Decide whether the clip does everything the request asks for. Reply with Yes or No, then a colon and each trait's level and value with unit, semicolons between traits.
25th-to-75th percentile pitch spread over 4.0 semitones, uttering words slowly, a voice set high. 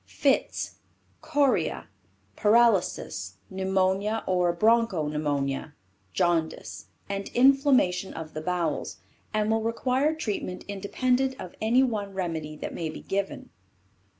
Yes: average, 5.3 semitones; slow, 110 wpm; high, 195 Hz